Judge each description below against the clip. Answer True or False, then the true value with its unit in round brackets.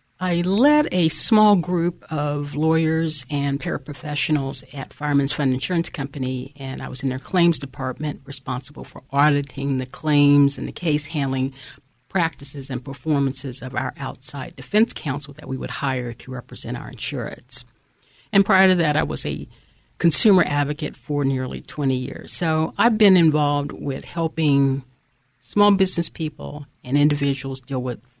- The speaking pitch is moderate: True (145 Hz)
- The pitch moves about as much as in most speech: True (3.2 semitones)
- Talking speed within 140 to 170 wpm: True (155 wpm)